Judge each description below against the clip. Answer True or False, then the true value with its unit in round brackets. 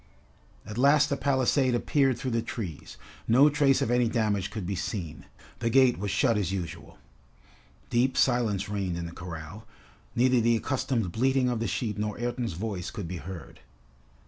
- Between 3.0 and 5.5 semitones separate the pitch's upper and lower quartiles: True (4.7 semitones)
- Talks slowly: False (170 wpm)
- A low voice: True (115 Hz)